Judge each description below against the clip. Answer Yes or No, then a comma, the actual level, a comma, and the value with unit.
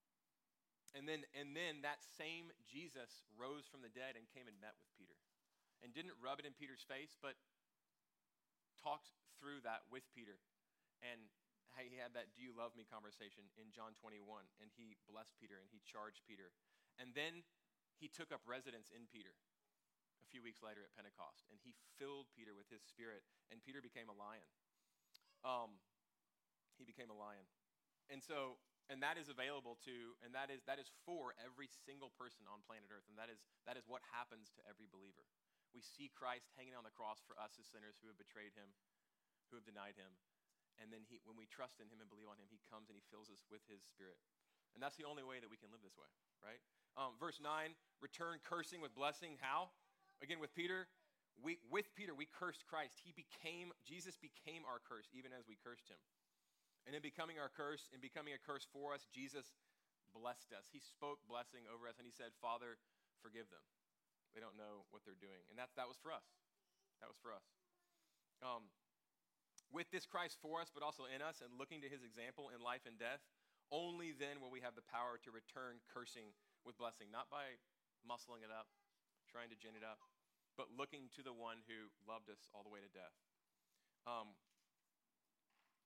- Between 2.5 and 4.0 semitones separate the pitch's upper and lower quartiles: No, average, 4.6 semitones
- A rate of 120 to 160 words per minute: No, average, 200 wpm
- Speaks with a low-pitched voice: Yes, low, 120 Hz